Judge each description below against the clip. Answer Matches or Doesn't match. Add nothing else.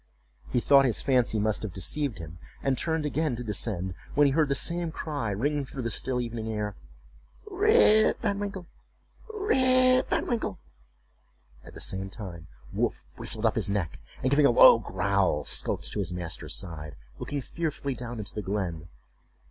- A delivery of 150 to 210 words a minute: Matches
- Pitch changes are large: Matches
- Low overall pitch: Matches